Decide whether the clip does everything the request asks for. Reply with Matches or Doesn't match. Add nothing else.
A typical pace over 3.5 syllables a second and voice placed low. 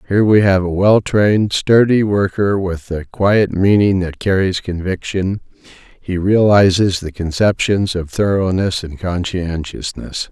Matches